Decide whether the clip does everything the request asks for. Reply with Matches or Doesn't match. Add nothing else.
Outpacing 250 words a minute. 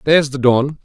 Doesn't match